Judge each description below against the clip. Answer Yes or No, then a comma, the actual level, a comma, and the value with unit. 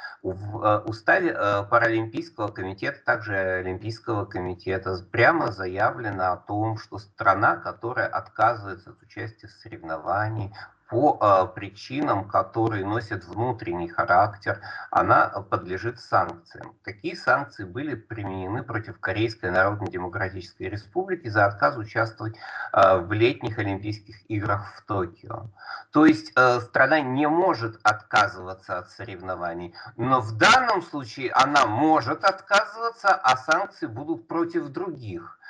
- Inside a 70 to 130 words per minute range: Yes, slow, 110 wpm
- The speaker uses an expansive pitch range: No, average, 3.4 semitones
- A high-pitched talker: No, low, 110 Hz